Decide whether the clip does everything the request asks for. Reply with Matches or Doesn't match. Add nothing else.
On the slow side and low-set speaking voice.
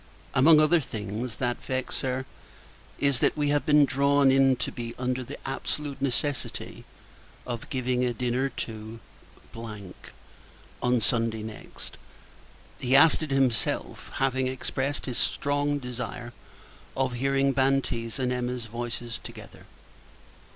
Matches